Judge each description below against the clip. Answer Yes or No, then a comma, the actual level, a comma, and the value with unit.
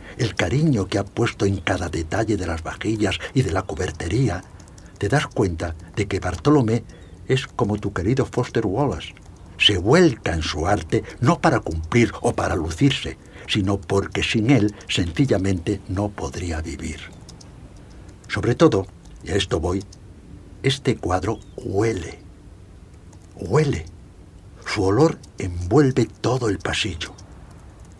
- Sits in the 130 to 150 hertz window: No, very low, 95 Hz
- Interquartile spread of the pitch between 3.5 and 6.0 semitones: Yes, average, 4.0 semitones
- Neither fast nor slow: Yes, average, 135 wpm